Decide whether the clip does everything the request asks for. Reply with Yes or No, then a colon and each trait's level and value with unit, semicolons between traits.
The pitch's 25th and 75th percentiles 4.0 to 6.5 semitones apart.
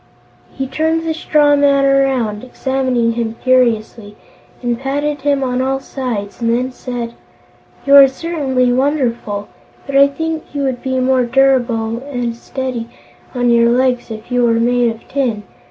No: average, 2.7 semitones